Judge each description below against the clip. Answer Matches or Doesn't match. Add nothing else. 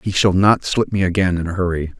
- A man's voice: Matches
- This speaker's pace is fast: Matches